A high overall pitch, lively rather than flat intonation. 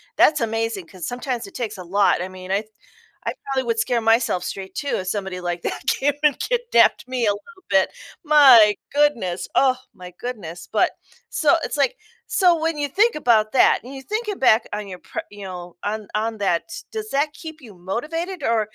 Yes: high, 230 Hz; wide, 7.0 semitones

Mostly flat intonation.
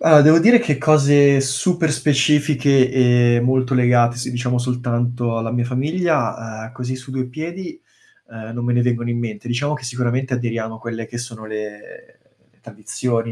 No: average, 3.1 semitones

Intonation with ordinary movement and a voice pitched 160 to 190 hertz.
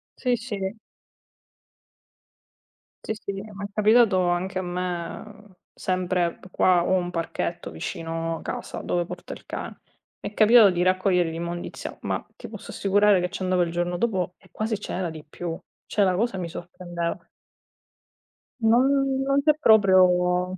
Yes: average, 3.0 semitones; medium, 185 Hz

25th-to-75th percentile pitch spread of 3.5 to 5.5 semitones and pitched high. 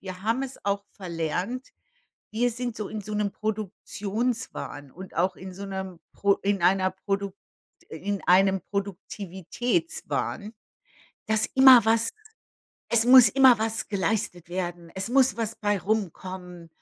No: average, 3.1 semitones; high, 200 Hz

